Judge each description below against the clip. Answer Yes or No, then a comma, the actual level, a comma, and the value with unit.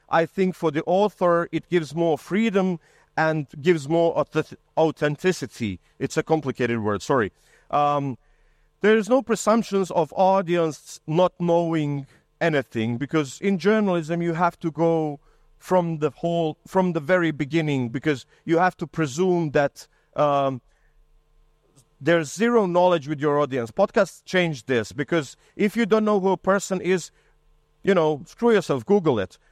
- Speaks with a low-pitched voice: No, medium, 165 Hz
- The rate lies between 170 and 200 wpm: No, average, 150 wpm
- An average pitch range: Yes, average, 3.8 semitones